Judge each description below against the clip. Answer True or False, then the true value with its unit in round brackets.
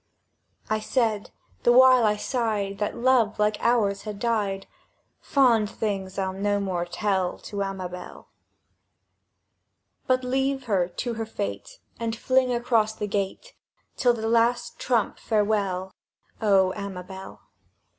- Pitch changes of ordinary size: True (3.3 semitones)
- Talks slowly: True (125 wpm)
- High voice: True (215 Hz)